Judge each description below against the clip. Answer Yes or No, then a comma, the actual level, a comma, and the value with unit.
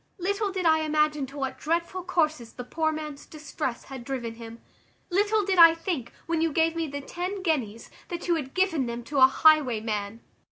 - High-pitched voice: Yes, very high, 310 Hz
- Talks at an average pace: Yes, average, 195 wpm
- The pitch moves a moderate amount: Yes, average, 4.7 semitones